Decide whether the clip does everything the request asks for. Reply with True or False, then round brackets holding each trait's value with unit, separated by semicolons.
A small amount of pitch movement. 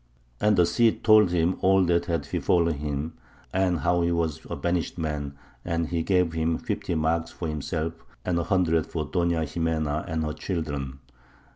True (2.1 semitones)